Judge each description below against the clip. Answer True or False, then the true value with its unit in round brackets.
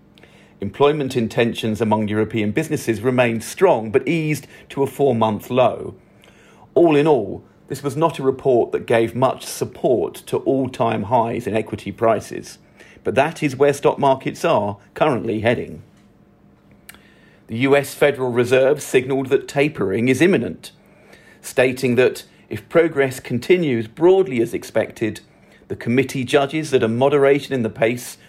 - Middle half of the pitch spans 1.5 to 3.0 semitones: False (3.8 semitones)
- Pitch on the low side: True (130 Hz)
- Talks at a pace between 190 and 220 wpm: False (145 wpm)